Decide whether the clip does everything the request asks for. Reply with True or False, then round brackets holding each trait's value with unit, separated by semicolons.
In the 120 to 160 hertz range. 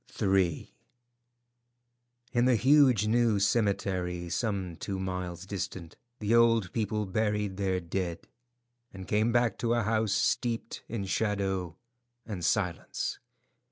False (100 Hz)